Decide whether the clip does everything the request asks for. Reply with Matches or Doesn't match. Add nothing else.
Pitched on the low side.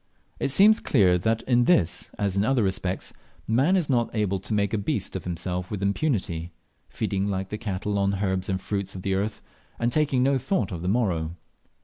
Matches